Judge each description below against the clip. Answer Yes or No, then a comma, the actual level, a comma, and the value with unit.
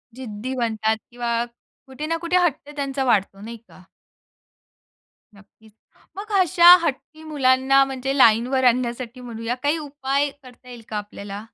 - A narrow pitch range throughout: No, average, 3.6 semitones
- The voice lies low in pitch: No, very high, 255 Hz